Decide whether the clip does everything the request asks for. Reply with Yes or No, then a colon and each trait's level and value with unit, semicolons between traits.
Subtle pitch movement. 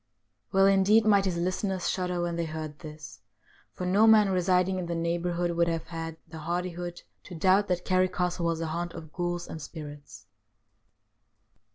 Yes: narrow, 2.0 semitones